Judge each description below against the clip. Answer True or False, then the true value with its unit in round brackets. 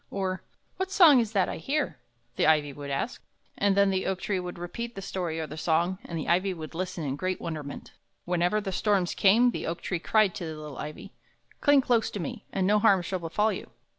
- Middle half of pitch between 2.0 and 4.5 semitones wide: True (4.1 semitones)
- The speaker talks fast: True (225 wpm)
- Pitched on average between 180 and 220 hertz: True (185 Hz)